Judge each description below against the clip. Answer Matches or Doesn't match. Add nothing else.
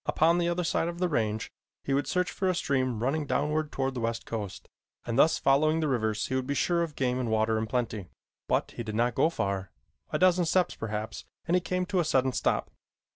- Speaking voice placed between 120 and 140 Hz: Matches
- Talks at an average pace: Doesn't match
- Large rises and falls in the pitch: Matches